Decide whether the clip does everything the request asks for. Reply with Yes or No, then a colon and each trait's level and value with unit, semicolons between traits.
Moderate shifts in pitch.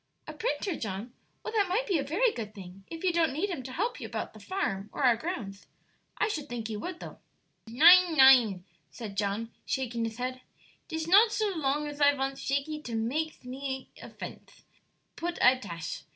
No: wide, 6.9 semitones